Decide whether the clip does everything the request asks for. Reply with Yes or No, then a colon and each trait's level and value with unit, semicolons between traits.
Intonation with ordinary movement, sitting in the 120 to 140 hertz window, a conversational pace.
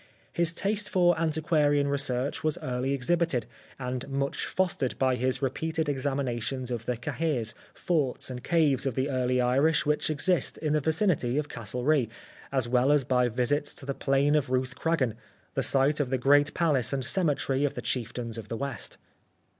Yes: average, 3.3 semitones; low, 135 Hz; average, 170 wpm